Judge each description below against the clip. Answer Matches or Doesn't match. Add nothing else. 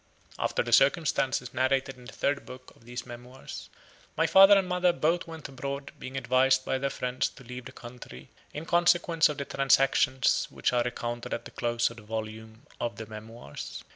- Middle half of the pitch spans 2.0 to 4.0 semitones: Matches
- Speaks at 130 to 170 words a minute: Doesn't match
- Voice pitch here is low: Matches